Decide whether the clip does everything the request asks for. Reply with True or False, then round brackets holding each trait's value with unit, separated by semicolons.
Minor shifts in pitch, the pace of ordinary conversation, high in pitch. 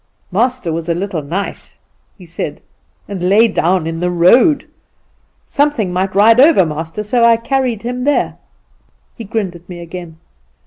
False (5.2 semitones; 155 wpm; 195 Hz)